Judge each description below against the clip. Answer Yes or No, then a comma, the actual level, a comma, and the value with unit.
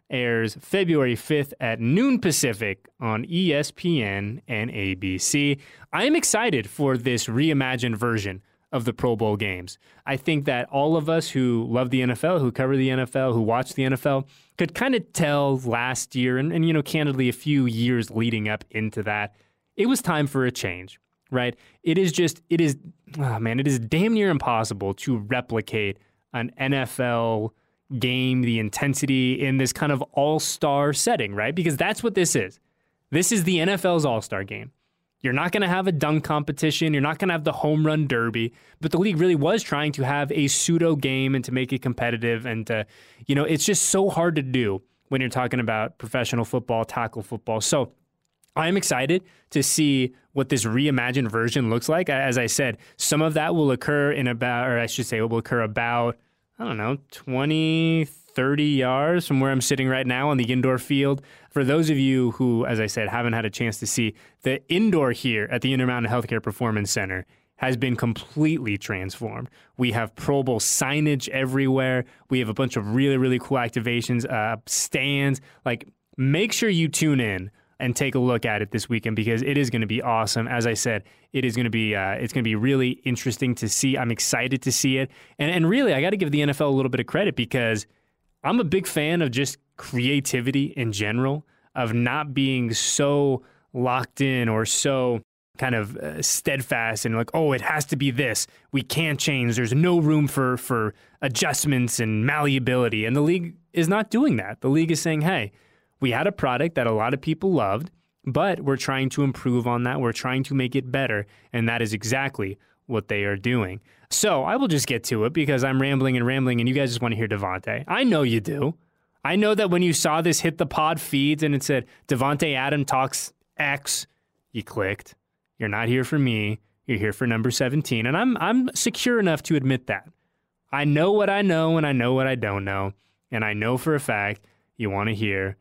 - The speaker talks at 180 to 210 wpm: Yes, fast, 205 wpm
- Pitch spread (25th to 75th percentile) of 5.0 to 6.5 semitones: No, average, 4.3 semitones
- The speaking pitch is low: Yes, low, 130 Hz